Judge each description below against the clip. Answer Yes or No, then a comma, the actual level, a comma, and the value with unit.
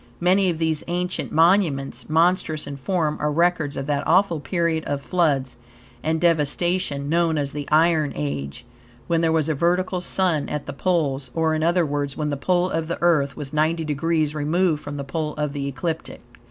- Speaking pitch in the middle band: Yes, medium, 155 Hz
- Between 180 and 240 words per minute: Yes, average, 190 wpm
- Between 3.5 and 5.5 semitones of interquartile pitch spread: No, average, 3.0 semitones